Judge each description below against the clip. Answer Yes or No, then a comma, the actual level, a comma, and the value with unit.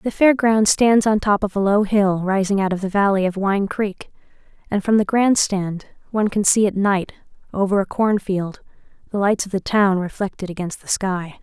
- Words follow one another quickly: Yes, fast, 210 wpm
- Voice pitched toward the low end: No, high, 200 Hz